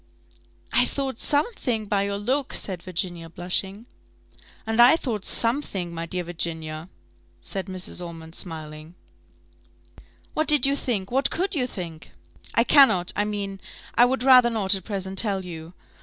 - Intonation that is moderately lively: No, wide, 5.9 semitones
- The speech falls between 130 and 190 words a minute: Yes, average, 150 wpm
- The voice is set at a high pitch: Yes, high, 195 Hz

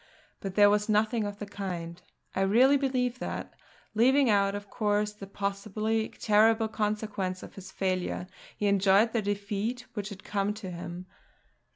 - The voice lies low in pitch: No, high, 205 Hz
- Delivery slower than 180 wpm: Yes, average, 160 wpm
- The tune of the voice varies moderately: No, narrow, 1.9 semitones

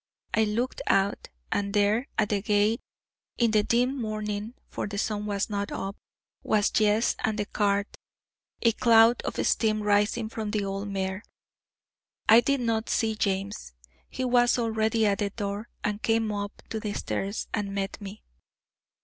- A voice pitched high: Yes, high, 210 Hz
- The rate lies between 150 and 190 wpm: Yes, average, 165 wpm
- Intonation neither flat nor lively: No, narrow, 1.7 semitones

